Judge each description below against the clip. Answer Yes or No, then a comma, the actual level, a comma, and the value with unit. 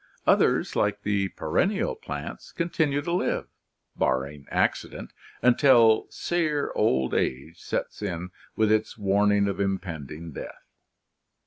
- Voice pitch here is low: Yes, low, 100 Hz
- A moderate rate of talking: No, slow, 120 wpm